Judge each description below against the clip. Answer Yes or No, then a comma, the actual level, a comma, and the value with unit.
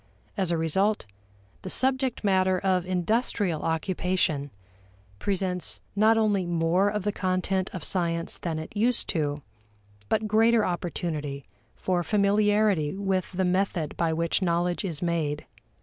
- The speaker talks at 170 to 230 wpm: No, slow, 135 wpm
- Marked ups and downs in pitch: No, average, 3.3 semitones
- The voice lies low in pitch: No, medium, 185 Hz